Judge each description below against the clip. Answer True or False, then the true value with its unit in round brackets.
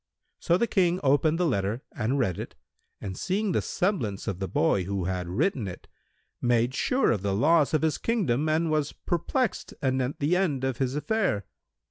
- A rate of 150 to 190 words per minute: True (185 wpm)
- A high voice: False (140 Hz)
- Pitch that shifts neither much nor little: False (8.3 semitones)